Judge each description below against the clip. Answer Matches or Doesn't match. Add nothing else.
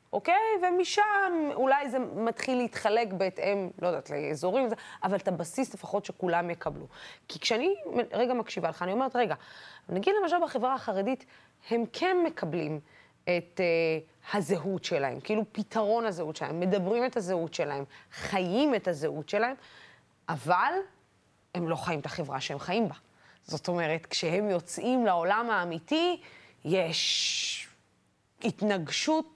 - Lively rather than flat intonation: Matches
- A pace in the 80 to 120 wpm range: Doesn't match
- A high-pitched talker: Matches